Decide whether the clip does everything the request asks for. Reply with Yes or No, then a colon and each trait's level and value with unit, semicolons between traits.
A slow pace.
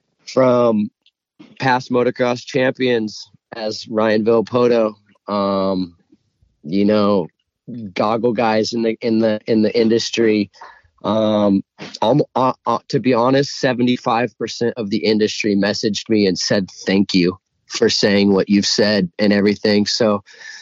Yes: slow, 130 wpm